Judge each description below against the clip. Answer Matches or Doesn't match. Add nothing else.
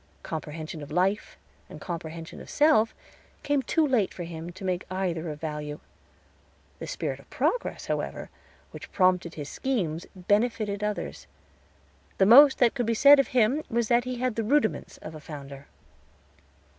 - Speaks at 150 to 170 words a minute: Matches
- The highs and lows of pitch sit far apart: Matches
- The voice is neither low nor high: Doesn't match